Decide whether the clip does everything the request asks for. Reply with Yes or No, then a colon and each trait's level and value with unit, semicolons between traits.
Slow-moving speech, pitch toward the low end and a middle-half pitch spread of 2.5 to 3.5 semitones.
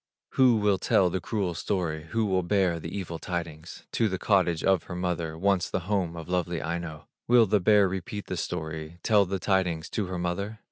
No: average, 200 wpm; very low, 90 Hz; average, 2.9 semitones